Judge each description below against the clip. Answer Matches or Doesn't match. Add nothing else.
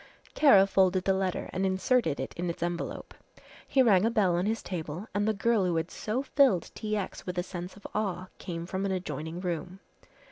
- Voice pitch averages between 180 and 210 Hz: Matches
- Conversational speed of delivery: Doesn't match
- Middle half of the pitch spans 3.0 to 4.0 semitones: Matches